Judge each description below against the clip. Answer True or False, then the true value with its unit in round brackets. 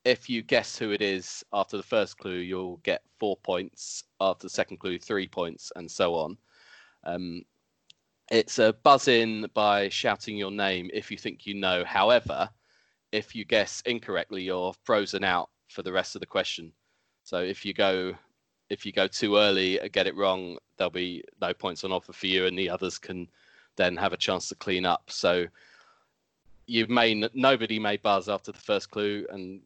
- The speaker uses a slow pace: False (190 wpm)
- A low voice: True (100 Hz)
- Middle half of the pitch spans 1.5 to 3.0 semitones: True (2.5 semitones)